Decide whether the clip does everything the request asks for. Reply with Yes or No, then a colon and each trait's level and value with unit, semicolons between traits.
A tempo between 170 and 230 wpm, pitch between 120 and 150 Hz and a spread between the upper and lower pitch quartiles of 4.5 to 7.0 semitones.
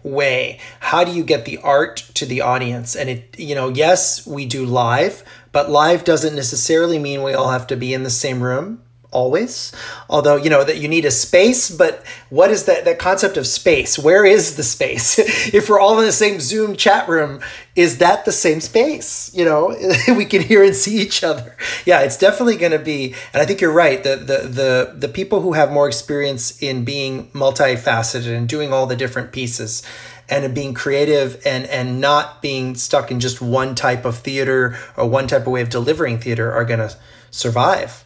Yes: fast, 205 wpm; medium, 140 Hz; wide, 5.4 semitones